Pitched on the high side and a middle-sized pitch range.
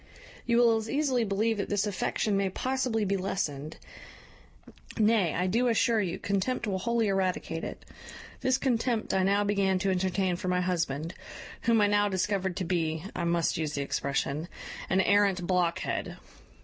Yes: high, 195 Hz; average, 3.5 semitones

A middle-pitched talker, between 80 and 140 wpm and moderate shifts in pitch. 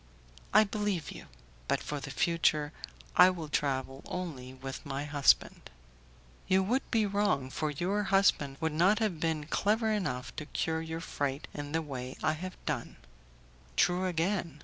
No: medium, 160 Hz; average, 160 wpm; average, 4.8 semitones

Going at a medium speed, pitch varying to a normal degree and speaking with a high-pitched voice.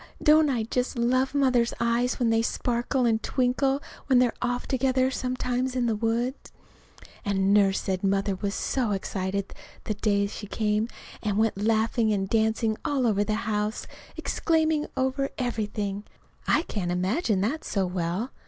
Yes: average, 155 wpm; average, 3.7 semitones; high, 225 Hz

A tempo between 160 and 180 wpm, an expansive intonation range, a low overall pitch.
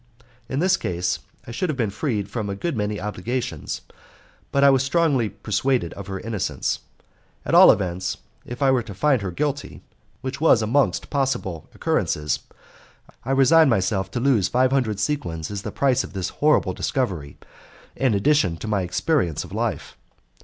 Yes: average, 170 wpm; wide, 6.0 semitones; low, 115 Hz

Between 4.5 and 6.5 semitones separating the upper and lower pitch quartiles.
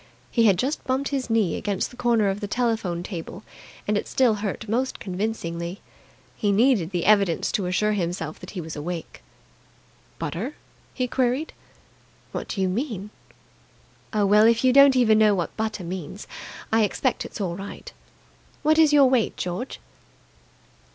Yes: average, 5.1 semitones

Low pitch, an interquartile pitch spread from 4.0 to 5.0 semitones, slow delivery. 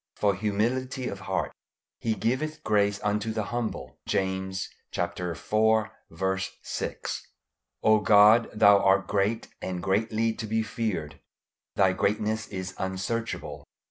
No: low, 105 Hz; narrow, 2.6 semitones; slow, 115 wpm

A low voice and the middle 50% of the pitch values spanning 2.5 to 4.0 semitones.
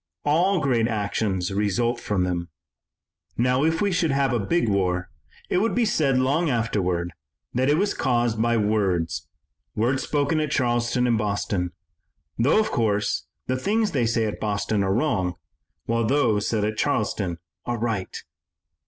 No: low, 115 Hz; wide, 5.4 semitones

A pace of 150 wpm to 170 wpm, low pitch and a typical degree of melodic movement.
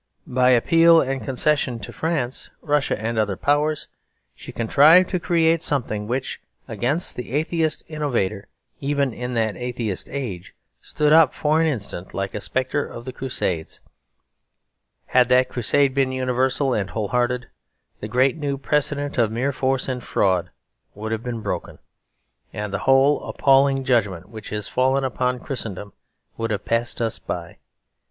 Yes: average, 155 wpm; low, 130 Hz; average, 4.1 semitones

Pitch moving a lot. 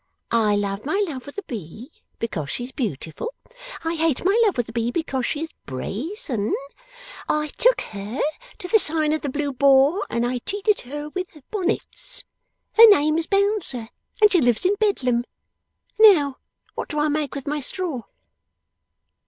Yes: wide, 7.3 semitones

